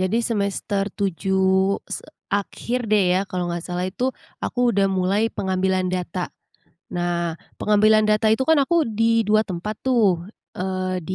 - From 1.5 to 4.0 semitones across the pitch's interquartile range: Yes, average, 2.7 semitones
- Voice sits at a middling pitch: No, high, 195 Hz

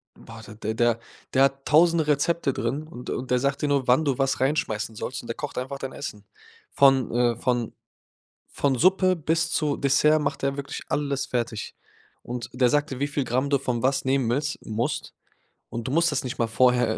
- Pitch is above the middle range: No, low, 135 Hz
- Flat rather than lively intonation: No, average, 3.0 semitones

